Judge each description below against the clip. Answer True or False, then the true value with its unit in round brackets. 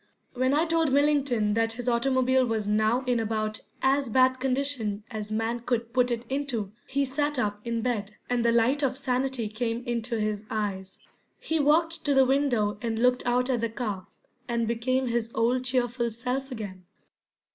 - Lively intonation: False (2.9 semitones)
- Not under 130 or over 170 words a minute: False (180 wpm)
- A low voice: False (245 Hz)